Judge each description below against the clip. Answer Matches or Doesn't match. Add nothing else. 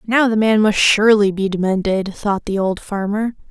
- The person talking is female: Matches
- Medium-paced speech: Matches